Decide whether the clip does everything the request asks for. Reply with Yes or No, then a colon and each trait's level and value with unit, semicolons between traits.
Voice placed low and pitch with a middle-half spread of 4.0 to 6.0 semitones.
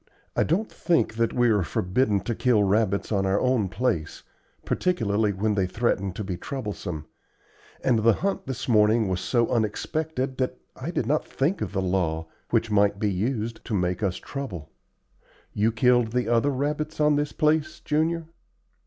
Yes: low, 115 Hz; average, 5.1 semitones